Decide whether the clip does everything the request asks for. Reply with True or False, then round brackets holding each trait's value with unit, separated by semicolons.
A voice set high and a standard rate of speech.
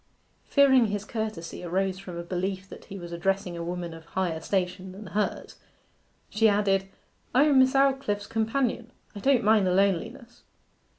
True (195 Hz; 170 wpm)